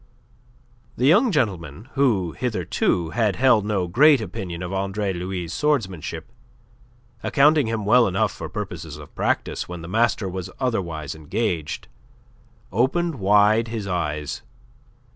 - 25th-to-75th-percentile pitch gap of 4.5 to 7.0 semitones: Yes, wide, 5.4 semitones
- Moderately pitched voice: No, low, 100 Hz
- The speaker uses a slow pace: Yes, slow, 125 wpm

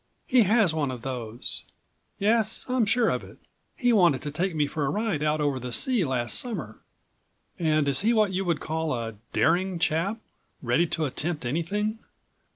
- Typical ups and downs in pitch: No, wide, 6.7 semitones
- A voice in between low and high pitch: Yes, medium, 160 Hz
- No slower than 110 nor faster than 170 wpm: No, average, 180 wpm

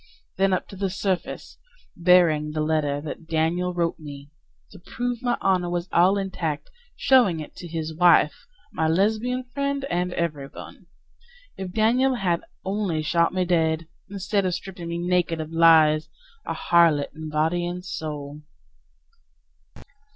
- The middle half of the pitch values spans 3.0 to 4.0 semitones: Yes, average, 3.3 semitones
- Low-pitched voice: No, medium, 175 Hz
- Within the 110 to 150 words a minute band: Yes, average, 145 wpm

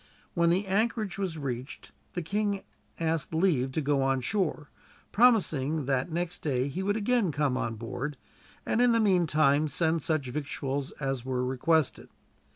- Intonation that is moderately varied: No, wide, 5.9 semitones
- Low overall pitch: No, medium, 155 Hz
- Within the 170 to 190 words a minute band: No, average, 160 wpm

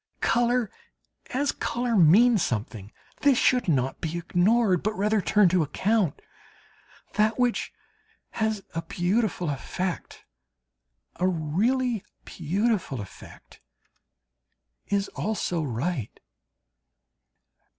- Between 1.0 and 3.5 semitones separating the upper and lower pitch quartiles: No, wide, 5.6 semitones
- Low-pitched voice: No, high, 195 Hz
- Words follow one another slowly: Yes, slow, 95 wpm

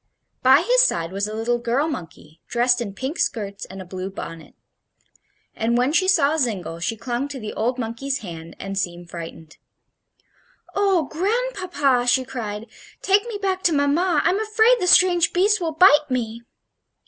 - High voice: Yes, very high, 255 Hz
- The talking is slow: No, average, 170 wpm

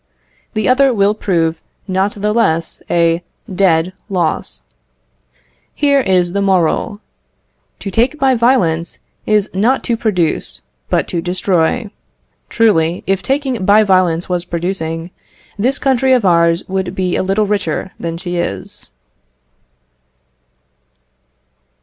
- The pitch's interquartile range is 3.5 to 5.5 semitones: Yes, average, 4.2 semitones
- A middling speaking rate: No, slow, 120 wpm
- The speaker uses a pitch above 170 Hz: Yes, high, 190 Hz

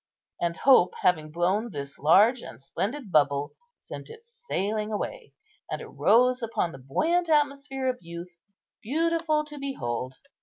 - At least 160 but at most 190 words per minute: No, average, 145 wpm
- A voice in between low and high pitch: No, high, 220 Hz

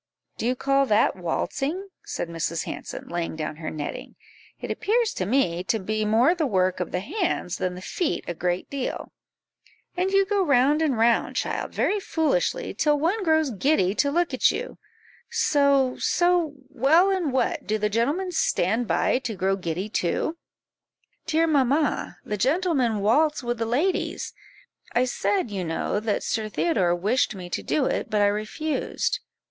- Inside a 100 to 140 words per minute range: No, average, 170 wpm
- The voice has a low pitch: No, very high, 255 Hz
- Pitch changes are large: Yes, wide, 8.0 semitones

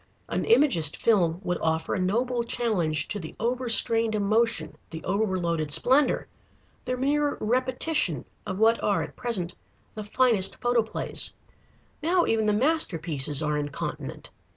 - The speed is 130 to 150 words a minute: Yes, slow, 135 wpm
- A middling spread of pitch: No, wide, 6.4 semitones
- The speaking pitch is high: Yes, high, 215 Hz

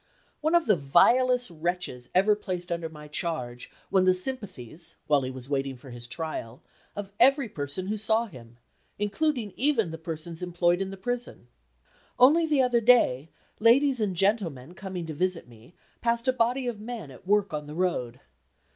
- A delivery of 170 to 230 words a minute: Yes, average, 175 wpm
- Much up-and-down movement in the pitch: Yes, wide, 7.6 semitones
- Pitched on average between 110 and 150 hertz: No, medium, 185 Hz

